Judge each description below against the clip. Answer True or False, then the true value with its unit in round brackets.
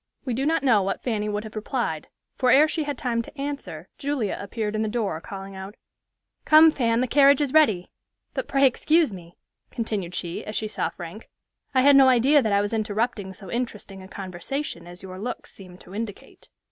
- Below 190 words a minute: False (205 wpm)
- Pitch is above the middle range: True (220 Hz)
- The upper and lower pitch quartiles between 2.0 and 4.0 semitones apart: False (5.5 semitones)